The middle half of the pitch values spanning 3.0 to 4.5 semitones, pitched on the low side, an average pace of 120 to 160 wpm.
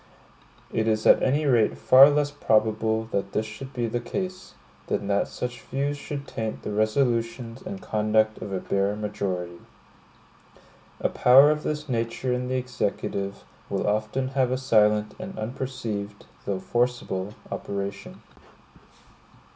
Yes: average, 3.8 semitones; low, 115 Hz; average, 140 wpm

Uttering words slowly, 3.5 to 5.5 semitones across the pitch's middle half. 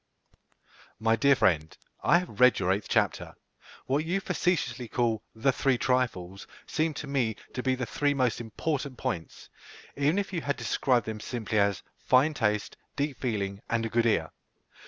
No: average, 165 wpm; average, 4.6 semitones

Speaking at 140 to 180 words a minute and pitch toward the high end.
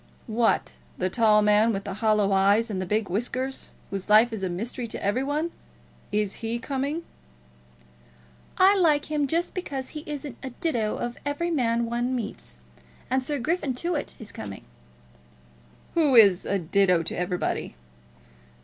Yes: average, 160 wpm; high, 235 Hz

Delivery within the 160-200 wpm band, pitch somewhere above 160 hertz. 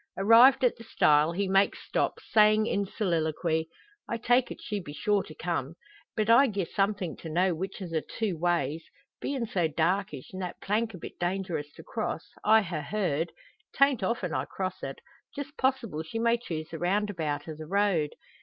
Yes: average, 190 wpm; high, 190 Hz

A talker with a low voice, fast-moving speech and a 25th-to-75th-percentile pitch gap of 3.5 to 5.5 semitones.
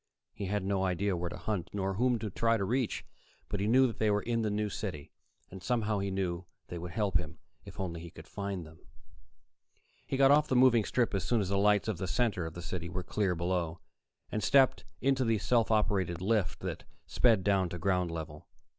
Yes: low, 100 Hz; fast, 225 wpm; average, 3.9 semitones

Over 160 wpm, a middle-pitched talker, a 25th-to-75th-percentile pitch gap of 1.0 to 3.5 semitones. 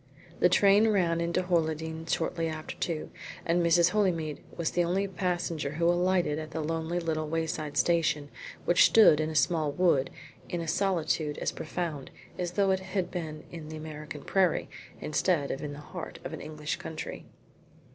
Yes: average, 170 wpm; medium, 165 Hz; narrow, 2.4 semitones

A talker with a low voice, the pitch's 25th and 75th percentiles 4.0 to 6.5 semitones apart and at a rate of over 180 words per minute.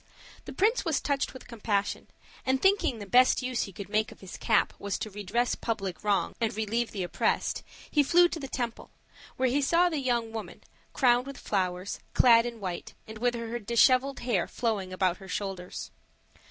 No: high, 230 Hz; average, 4.3 semitones; average, 190 wpm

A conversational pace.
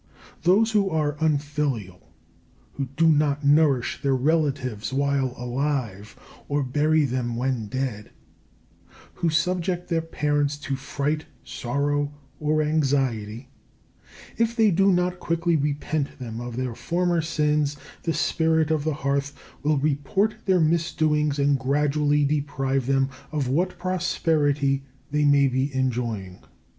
No: slow, 130 wpm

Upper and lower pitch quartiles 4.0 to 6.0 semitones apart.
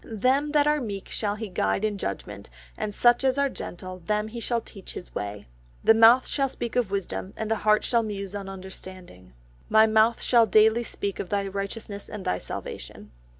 No: average, 3.3 semitones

